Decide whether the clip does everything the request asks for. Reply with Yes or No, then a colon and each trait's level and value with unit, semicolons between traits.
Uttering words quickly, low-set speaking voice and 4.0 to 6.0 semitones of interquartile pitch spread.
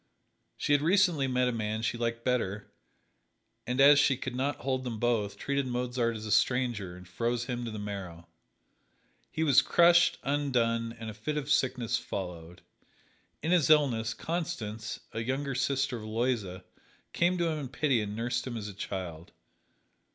No: average, 175 wpm; low, 120 Hz; average, 4.3 semitones